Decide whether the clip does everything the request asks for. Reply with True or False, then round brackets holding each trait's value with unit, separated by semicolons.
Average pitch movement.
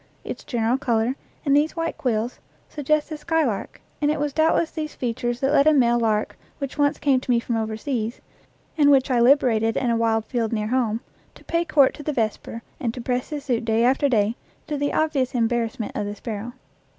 True (4.1 semitones)